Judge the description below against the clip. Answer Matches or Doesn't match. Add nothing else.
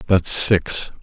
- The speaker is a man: Matches